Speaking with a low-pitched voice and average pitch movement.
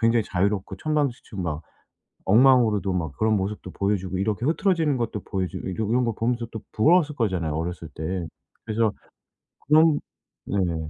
Yes: low, 105 Hz; average, 4.8 semitones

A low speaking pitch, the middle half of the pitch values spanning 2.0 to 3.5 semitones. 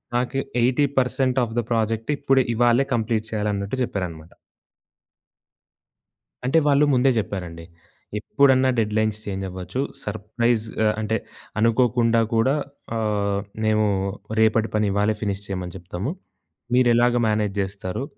Yes: low, 110 Hz; average, 3.2 semitones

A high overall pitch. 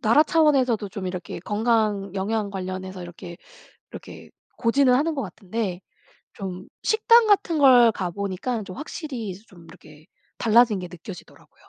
Yes: high, 210 Hz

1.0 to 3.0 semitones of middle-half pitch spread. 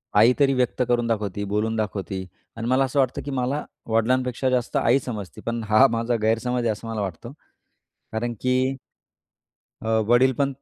Yes: narrow, 2.6 semitones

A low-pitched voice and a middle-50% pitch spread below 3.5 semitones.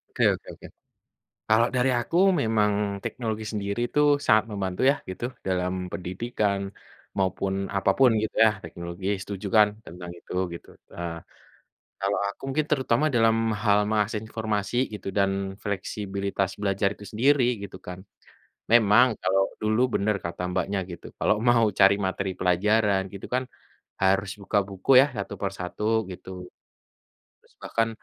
Yes: low, 100 Hz; average, 2.8 semitones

